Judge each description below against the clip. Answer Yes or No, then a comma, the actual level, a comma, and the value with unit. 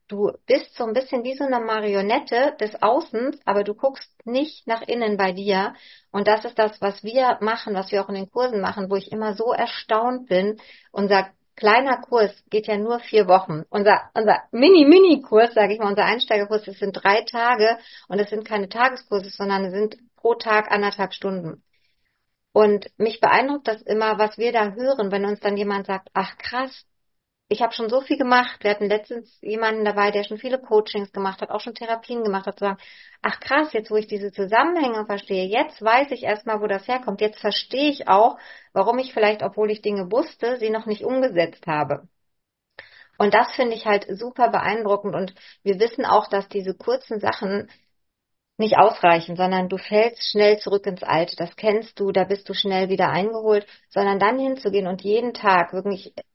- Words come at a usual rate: No, fast, 195 wpm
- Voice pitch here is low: No, high, 215 Hz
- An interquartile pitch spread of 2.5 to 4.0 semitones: Yes, average, 2.9 semitones